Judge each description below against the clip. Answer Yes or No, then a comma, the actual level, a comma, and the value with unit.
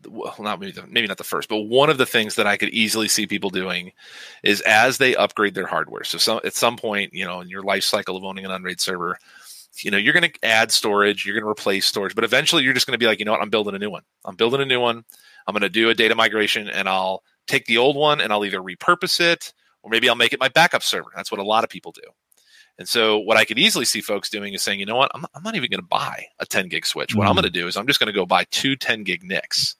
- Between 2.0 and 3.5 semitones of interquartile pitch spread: No, average, 4.1 semitones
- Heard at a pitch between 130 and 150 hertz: No, low, 105 Hz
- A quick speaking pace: Yes, fast, 300 wpm